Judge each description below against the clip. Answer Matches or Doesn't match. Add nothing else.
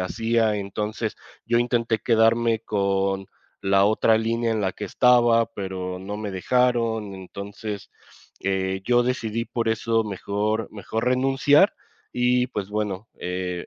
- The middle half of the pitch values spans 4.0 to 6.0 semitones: Doesn't match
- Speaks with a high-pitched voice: Doesn't match